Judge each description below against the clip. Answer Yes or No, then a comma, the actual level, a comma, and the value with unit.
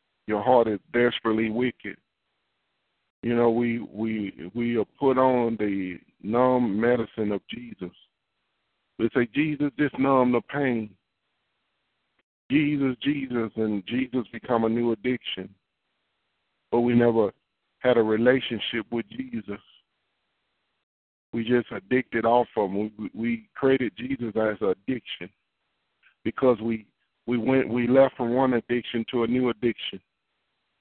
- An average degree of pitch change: No, narrow, 2.3 semitones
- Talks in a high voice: No, low, 120 Hz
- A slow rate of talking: Yes, slow, 130 wpm